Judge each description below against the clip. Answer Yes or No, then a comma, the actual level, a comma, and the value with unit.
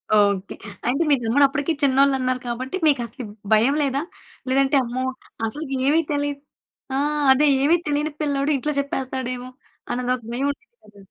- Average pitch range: No, narrow, 2.3 semitones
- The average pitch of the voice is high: Yes, very high, 270 Hz